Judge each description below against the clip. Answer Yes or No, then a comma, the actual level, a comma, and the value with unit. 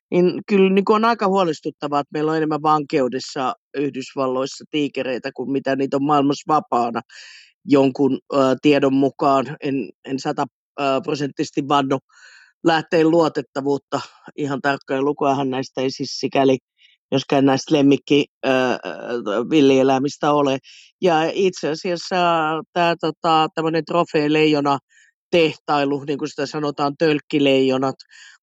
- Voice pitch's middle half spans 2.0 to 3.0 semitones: Yes, narrow, 2.4 semitones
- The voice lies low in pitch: No, medium, 145 Hz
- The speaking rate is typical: Yes, average, 110 wpm